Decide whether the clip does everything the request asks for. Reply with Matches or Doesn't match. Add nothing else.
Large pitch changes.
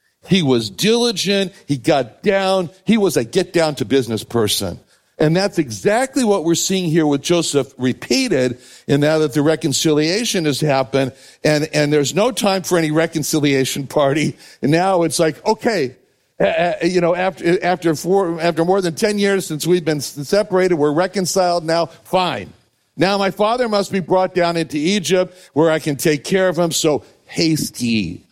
Doesn't match